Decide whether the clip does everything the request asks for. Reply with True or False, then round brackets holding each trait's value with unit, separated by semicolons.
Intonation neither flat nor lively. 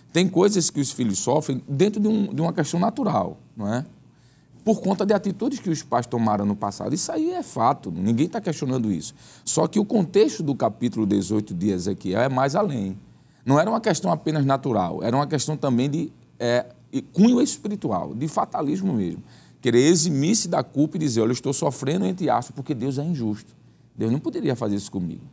False (7.3 semitones)